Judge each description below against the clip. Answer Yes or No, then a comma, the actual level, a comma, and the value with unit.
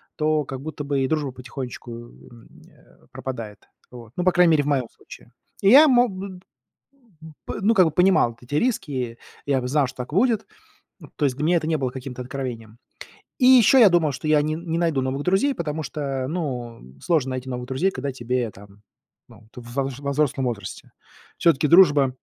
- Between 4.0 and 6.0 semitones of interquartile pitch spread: Yes, average, 4.8 semitones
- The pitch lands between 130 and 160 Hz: Yes, medium, 140 Hz